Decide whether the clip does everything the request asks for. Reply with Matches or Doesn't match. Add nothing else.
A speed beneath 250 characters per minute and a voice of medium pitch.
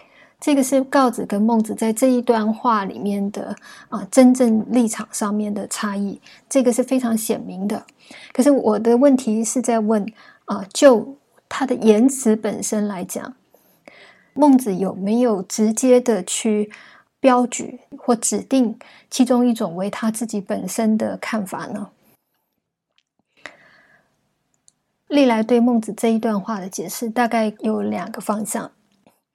Doesn't match